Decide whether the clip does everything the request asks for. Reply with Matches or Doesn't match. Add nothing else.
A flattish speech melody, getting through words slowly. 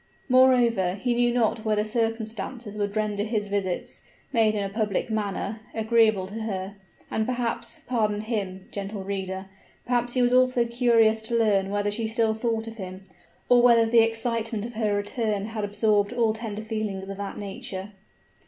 Doesn't match